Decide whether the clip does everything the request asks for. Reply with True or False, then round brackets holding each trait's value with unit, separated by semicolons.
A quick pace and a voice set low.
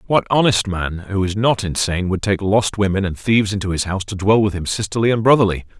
True (240 wpm; 100 Hz)